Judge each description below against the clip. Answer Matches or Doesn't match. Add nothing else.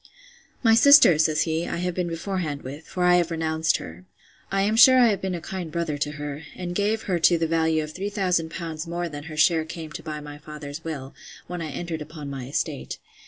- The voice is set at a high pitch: Doesn't match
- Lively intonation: Doesn't match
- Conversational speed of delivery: Doesn't match